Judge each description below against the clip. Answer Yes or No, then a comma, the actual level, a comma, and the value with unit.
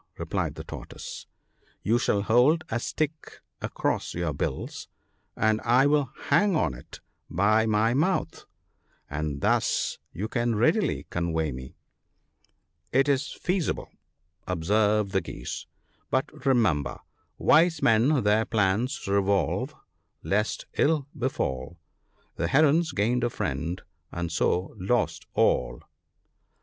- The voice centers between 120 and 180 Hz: No, low, 110 Hz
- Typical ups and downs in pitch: No, wide, 7.2 semitones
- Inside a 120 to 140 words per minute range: Yes, slow, 135 wpm